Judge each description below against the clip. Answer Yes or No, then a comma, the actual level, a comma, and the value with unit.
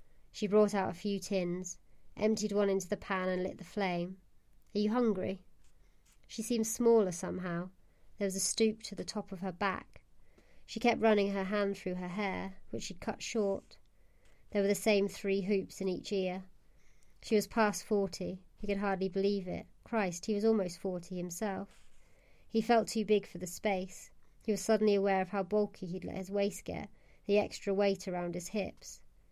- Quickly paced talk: No, average, 190 wpm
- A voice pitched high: Yes, high, 195 Hz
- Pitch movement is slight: Yes, narrow, 2.1 semitones